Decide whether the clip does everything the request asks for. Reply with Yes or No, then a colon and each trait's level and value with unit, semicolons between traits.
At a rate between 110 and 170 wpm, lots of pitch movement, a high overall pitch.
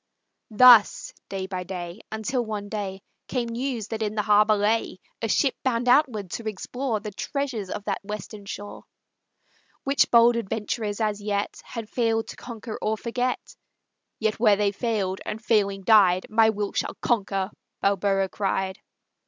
No: average, 155 wpm; narrow, 2.5 semitones; high, 215 Hz